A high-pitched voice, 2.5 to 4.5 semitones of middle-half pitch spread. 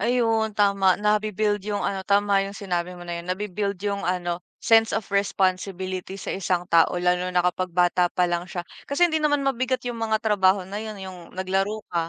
Yes: high, 195 Hz; average, 2.9 semitones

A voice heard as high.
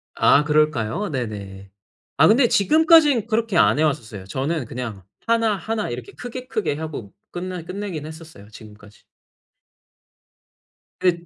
No: medium, 155 Hz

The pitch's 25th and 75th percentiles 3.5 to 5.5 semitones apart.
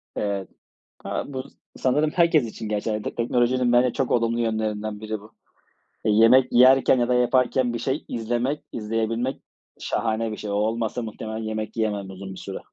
No: narrow, 2.5 semitones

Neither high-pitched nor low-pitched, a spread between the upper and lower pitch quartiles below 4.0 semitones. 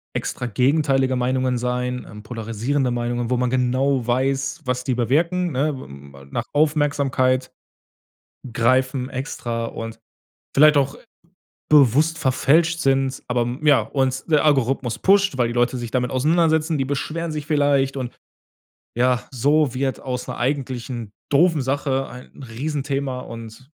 No: low, 130 Hz; average, 2.7 semitones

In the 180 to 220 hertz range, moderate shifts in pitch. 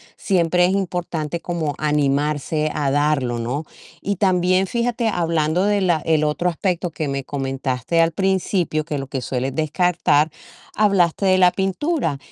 No: medium, 165 Hz; average, 4.0 semitones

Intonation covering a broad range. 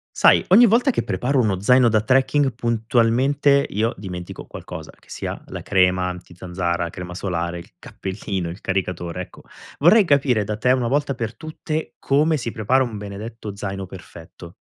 Yes: wide, 6.3 semitones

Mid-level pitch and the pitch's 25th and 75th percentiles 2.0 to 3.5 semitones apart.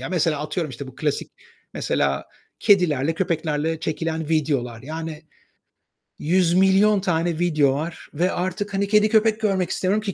No: medium, 165 Hz; average, 4.0 semitones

